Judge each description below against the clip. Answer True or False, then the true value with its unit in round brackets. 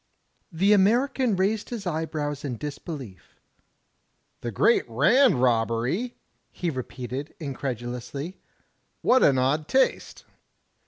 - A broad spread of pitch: True (7.9 semitones)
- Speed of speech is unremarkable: False (110 wpm)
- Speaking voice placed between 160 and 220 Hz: False (150 Hz)